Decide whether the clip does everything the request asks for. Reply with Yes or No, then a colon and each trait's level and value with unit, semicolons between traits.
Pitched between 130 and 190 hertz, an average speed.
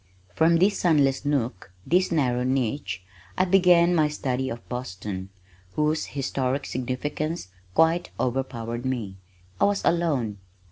No: low, 135 Hz; slow, 125 wpm